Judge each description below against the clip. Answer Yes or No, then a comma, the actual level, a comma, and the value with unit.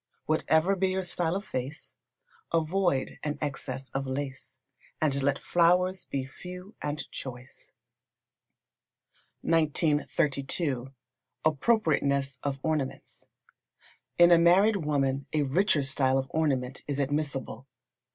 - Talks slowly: Yes, slow, 110 wpm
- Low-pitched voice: No, medium, 150 Hz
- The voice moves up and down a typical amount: Yes, average, 4.2 semitones